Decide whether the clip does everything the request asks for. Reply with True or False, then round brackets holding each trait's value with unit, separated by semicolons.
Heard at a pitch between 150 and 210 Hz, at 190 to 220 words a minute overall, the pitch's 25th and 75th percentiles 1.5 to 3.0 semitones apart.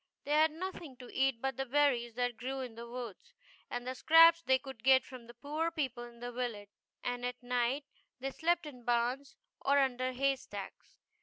False (255 Hz; 200 wpm; 2.6 semitones)